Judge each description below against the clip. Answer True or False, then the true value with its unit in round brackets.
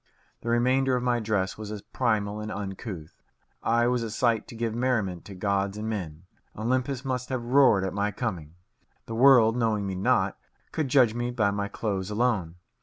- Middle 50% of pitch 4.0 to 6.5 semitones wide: False (3.5 semitones)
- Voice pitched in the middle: False (110 Hz)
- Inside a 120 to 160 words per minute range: False (185 wpm)